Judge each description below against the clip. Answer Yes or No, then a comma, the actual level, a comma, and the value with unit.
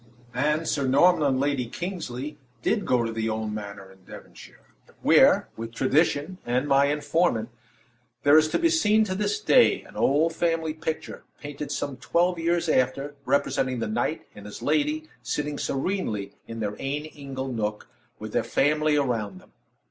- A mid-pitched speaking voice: Yes, medium, 145 Hz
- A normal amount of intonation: Yes, average, 4.8 semitones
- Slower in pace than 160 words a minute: No, average, 165 wpm